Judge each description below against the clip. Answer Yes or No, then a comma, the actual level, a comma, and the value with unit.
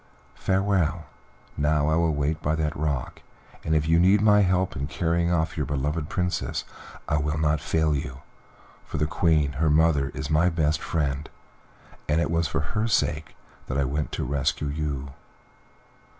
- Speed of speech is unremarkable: Yes, average, 170 wpm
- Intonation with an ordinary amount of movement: No, narrow, 2.3 semitones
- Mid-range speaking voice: No, very low, 75 Hz